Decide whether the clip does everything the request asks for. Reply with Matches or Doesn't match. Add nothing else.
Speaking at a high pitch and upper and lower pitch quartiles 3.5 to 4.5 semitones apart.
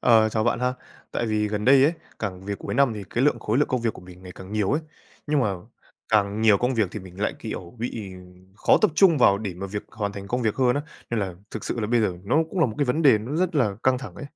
Doesn't match